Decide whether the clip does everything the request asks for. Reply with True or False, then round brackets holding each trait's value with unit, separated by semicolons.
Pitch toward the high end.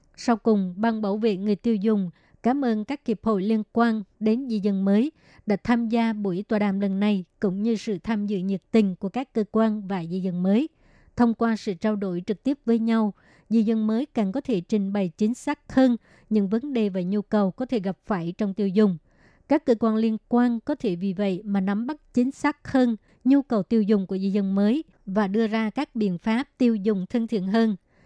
True (220 Hz)